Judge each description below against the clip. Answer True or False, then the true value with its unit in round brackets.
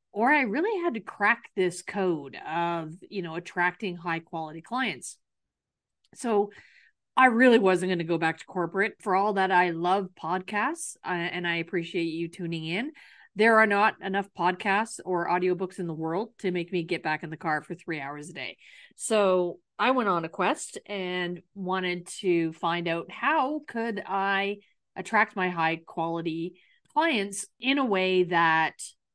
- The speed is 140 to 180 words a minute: True (175 wpm)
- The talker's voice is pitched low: False (185 Hz)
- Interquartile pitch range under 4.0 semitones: True (3.4 semitones)